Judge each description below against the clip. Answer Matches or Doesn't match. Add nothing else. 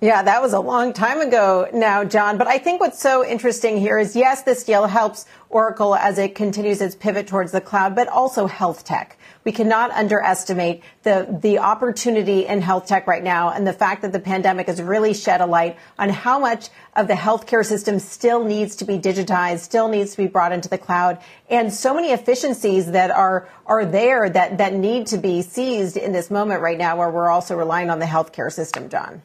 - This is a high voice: Matches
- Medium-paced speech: Doesn't match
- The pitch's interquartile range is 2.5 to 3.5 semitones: Matches